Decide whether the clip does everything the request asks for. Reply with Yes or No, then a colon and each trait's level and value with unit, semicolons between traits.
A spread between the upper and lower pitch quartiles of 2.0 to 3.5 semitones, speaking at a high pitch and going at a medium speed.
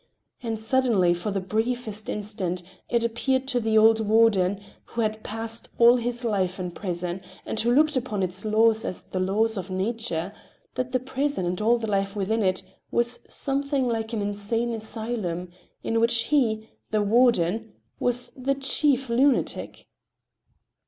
Yes: average, 3.2 semitones; high, 225 Hz; average, 160 wpm